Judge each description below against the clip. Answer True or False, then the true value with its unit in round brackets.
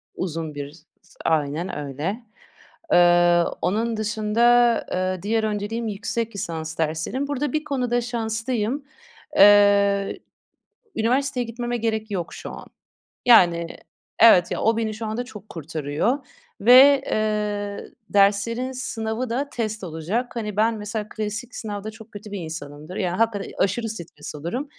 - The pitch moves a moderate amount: True (4.3 semitones)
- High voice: True (215 Hz)